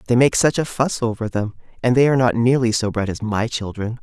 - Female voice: No, male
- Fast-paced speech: Yes, fast, 255 wpm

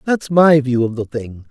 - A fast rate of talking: Yes, fast, 240 wpm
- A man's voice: Yes, male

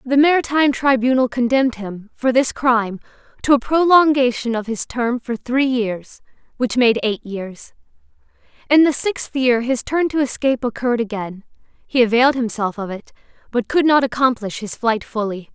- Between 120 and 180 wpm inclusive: Yes, average, 165 wpm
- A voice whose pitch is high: Yes, high, 245 Hz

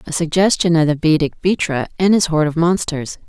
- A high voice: No, medium, 165 Hz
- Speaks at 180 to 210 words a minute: Yes, average, 200 wpm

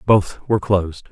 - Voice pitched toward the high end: No, low, 100 Hz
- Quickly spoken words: No, average, 160 wpm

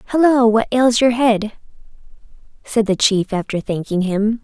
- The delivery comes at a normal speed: Yes, average, 150 wpm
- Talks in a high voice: Yes, high, 225 Hz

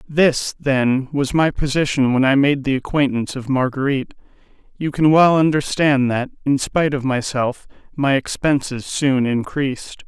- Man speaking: Yes, male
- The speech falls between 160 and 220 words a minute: No, average, 150 wpm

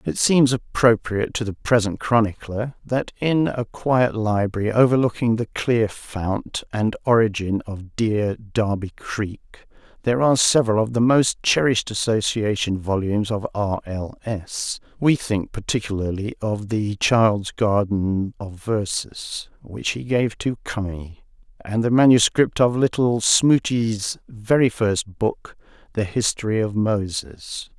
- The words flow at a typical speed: No, slow, 130 wpm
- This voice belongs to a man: Yes, male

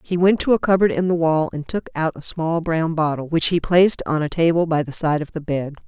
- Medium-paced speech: No, fast, 275 wpm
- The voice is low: No, medium, 165 Hz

